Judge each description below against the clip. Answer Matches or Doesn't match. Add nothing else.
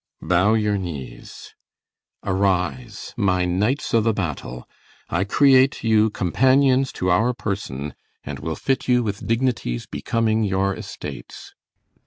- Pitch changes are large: Doesn't match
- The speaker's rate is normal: Doesn't match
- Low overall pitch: Matches